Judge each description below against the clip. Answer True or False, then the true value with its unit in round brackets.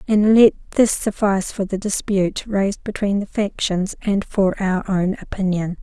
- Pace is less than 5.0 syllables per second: True (4.8 syllables/s)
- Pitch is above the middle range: True (200 Hz)